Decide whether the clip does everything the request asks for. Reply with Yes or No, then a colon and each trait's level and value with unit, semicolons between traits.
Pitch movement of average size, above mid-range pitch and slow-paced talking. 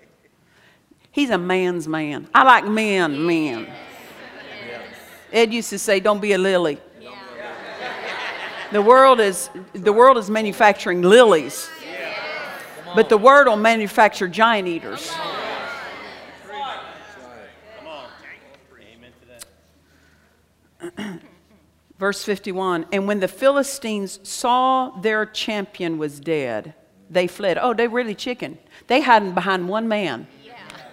Yes: average, 4.5 semitones; high, 205 Hz; slow, 105 wpm